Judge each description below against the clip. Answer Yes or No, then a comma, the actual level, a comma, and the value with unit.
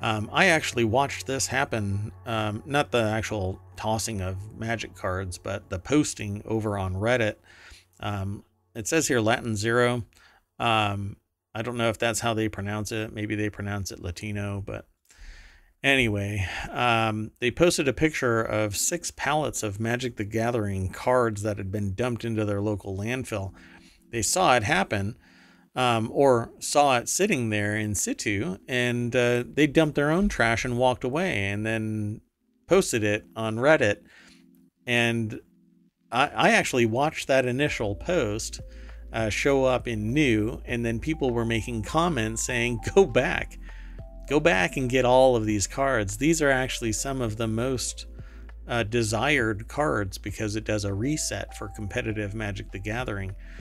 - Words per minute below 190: Yes, average, 160 wpm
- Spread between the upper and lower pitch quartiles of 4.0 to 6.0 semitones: No, average, 3.3 semitones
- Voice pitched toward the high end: No, low, 110 Hz